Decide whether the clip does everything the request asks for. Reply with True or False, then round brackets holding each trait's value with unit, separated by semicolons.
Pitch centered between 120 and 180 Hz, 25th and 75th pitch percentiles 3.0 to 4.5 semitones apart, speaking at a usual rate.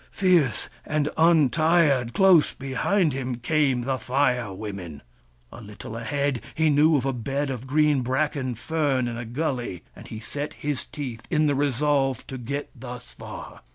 True (135 Hz; 3.7 semitones; 160 wpm)